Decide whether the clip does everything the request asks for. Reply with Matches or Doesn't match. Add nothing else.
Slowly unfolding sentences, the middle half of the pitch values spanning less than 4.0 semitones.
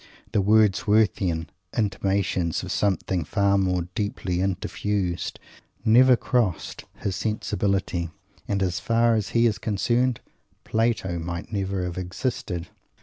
Matches